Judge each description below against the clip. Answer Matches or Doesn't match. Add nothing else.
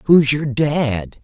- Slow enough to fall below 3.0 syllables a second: Matches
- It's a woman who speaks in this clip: Doesn't match